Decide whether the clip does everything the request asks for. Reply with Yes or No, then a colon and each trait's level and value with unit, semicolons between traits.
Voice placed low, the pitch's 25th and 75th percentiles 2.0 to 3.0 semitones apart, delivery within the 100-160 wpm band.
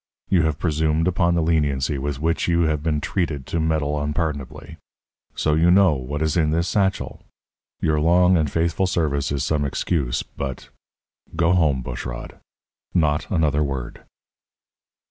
Yes: very low, 80 Hz; average, 2.7 semitones; average, 150 wpm